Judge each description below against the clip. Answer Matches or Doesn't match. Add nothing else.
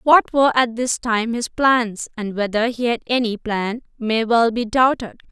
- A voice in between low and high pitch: Doesn't match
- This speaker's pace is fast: Doesn't match